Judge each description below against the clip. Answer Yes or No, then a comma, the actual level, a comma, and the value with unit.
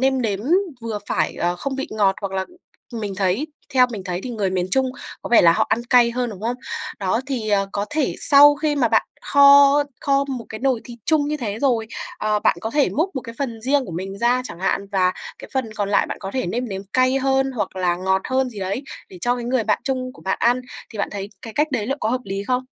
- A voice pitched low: No, high, 235 Hz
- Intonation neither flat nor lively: Yes, average, 5.0 semitones